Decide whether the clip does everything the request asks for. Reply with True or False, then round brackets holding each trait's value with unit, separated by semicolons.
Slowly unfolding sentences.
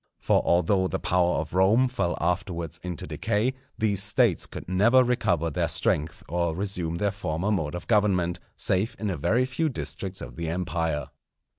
False (170 wpm)